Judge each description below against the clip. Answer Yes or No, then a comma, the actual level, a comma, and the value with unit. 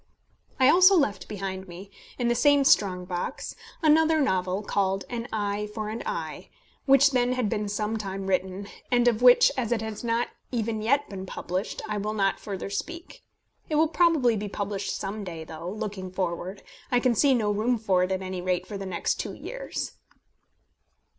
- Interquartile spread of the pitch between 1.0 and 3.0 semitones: No, average, 4.3 semitones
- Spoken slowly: No, average, 185 wpm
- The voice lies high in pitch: Yes, high, 210 Hz